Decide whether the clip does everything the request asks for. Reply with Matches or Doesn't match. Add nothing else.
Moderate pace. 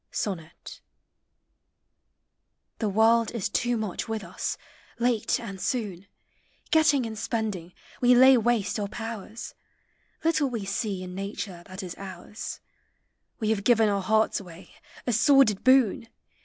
Doesn't match